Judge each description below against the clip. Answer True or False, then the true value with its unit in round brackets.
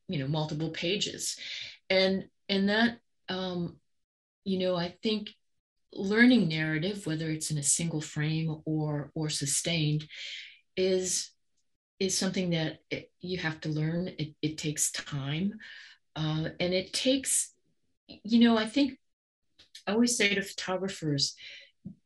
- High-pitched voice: False (180 Hz)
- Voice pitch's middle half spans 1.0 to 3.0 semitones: False (4.0 semitones)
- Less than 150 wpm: True (135 wpm)